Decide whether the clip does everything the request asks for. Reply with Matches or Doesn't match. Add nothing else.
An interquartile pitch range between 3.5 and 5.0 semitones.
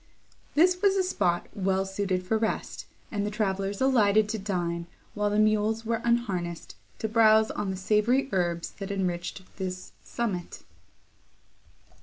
Doesn't match